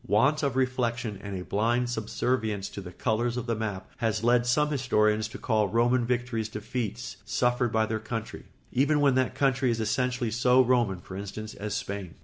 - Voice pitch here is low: Yes, low, 115 Hz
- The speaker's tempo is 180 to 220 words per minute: Yes, average, 185 wpm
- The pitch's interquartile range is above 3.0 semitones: No, average, 2.7 semitones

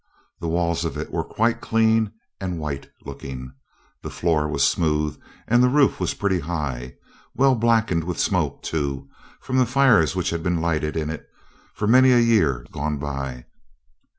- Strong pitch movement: Yes, wide, 7.1 semitones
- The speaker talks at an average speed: Yes, average, 170 wpm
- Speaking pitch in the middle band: No, very low, 85 Hz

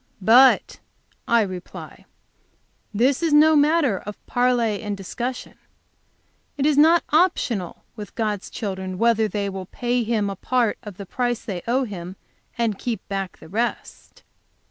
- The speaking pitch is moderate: No, high, 225 Hz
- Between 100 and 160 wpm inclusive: Yes, average, 145 wpm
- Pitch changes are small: No, average, 4.2 semitones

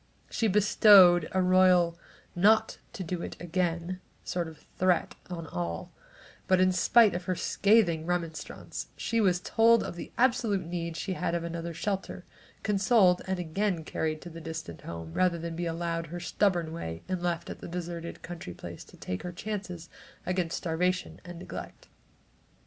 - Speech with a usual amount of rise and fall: No, narrow, 2.0 semitones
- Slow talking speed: No, average, 165 wpm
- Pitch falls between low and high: Yes, medium, 175 Hz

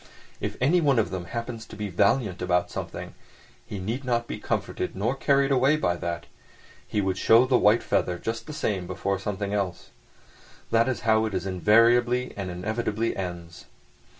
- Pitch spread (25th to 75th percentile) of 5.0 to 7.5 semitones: No, average, 4.6 semitones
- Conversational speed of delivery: Yes, average, 170 wpm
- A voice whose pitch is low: Yes, low, 105 Hz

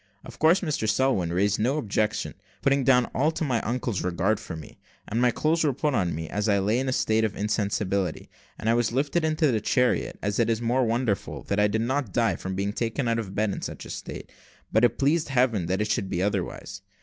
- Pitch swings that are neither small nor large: Yes, average, 4.6 semitones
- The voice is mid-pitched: No, low, 110 Hz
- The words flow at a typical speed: No, fast, 240 wpm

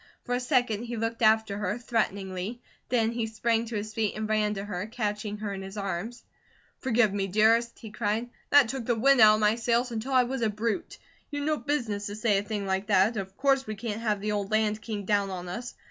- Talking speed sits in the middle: No, fast, 235 wpm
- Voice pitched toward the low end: No, high, 220 Hz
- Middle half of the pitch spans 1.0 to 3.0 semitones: Yes, narrow, 2.5 semitones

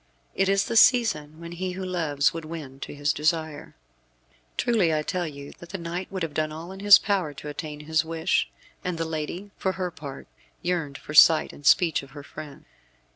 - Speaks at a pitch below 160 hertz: No, medium, 165 Hz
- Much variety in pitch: No, average, 3.5 semitones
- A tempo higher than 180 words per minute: Yes, fast, 205 wpm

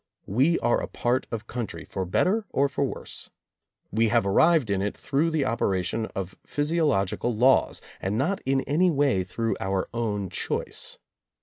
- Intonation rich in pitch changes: Yes, wide, 6.3 semitones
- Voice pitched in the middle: No, low, 120 Hz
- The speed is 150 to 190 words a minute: Yes, average, 170 wpm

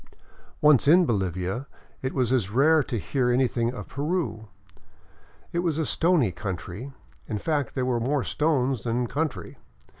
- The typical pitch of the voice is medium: No, low, 130 Hz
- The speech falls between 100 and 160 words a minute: Yes, average, 150 wpm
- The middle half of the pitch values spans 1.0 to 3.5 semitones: No, average, 4.7 semitones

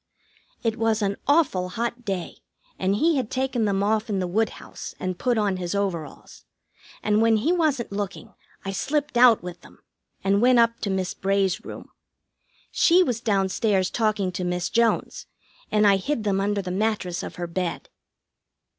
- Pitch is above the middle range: Yes, high, 205 Hz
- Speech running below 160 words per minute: No, average, 175 wpm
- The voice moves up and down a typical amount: Yes, average, 3.6 semitones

